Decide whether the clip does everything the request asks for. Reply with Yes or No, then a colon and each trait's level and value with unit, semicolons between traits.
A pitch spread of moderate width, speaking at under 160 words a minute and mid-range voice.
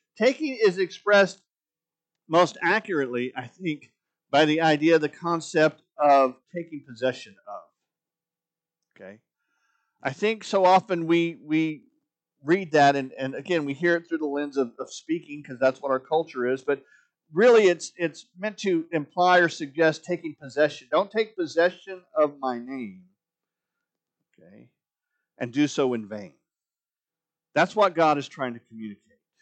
Yes: average, 4.2 semitones; average, 150 wpm; medium, 165 Hz